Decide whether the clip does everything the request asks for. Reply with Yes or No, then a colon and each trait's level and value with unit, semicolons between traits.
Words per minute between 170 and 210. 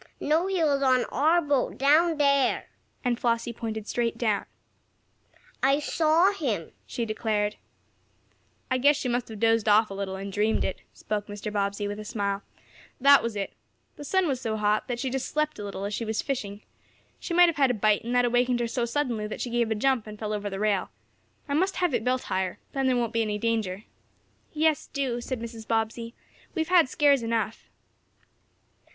Yes: average, 200 wpm